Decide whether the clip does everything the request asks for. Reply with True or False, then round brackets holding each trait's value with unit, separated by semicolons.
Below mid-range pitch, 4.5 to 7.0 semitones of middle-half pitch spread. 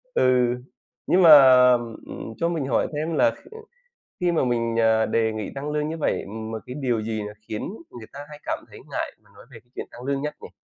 True (130 Hz; 4.9 semitones)